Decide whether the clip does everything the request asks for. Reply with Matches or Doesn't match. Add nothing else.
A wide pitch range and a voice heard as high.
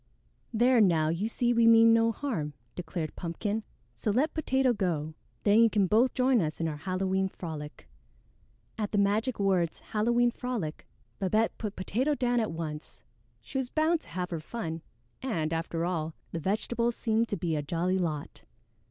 Matches